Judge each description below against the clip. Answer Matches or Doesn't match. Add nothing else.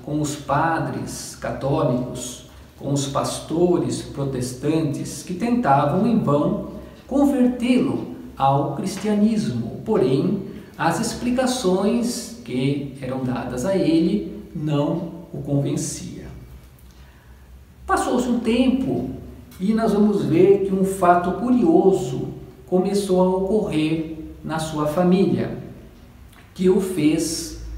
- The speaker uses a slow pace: Matches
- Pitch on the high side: Doesn't match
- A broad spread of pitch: Matches